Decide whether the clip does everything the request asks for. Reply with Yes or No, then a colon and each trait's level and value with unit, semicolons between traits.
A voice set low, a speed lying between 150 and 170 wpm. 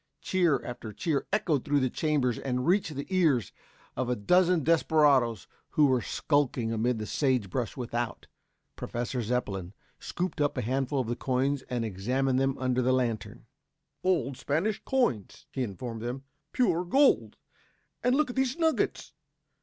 Yes: low, 130 Hz; average, 155 wpm